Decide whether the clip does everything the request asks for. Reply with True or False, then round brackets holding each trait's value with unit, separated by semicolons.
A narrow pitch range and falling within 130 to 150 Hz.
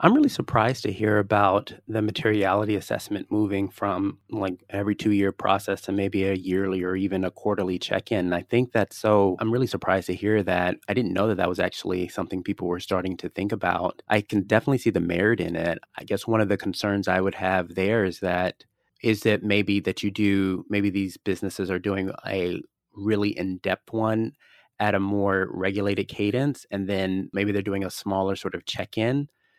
False (2.1 semitones; 100 Hz)